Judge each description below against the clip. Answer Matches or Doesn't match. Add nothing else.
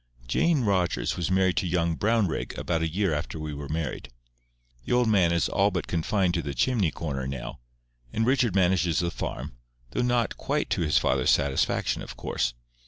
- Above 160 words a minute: Matches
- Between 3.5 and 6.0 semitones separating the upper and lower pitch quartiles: Matches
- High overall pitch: Doesn't match